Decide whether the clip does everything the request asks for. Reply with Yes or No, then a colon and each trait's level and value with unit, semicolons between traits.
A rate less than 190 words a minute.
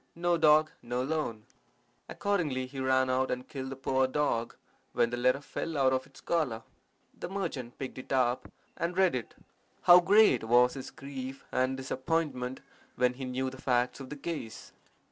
Yes: average, 175 wpm